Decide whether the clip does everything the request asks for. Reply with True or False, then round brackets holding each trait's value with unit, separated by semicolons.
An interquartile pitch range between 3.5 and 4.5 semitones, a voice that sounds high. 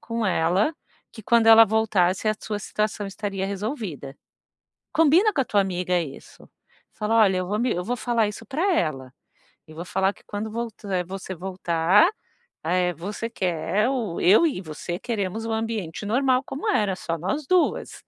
True (4.1 semitones; 205 Hz)